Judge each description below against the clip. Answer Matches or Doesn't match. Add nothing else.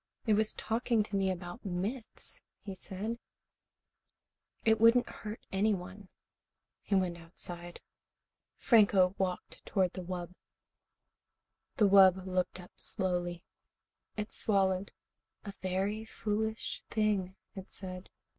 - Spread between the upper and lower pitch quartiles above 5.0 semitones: Doesn't match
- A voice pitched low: Doesn't match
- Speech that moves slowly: Matches